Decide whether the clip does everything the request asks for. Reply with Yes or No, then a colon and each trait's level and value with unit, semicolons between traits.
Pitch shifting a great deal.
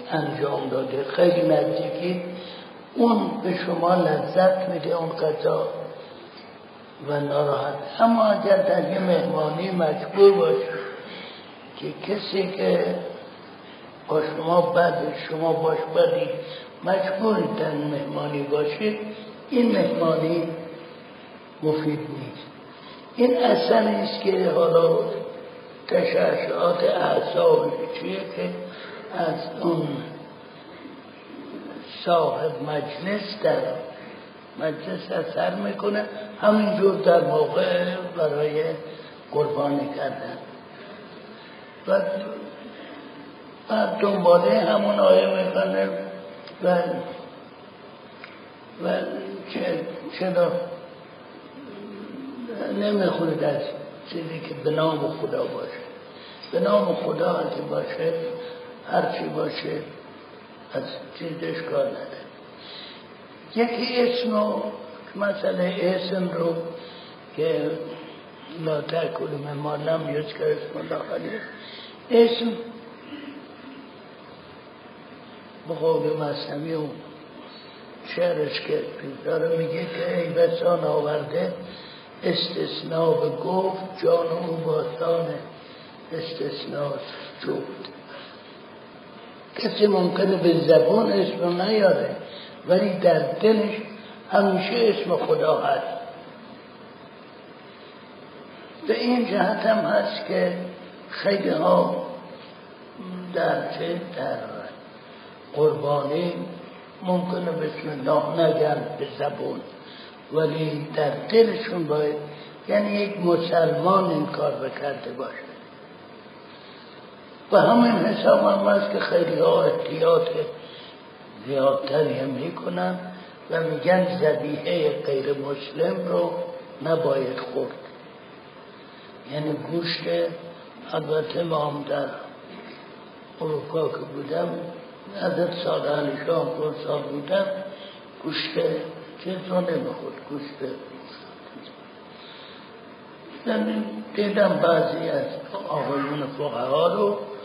Yes: wide, 6.6 semitones